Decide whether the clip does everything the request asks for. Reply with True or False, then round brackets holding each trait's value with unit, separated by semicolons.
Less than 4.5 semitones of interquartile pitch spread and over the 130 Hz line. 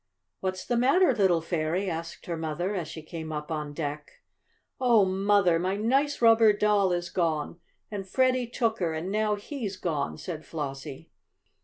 False (4.9 semitones; 185 Hz)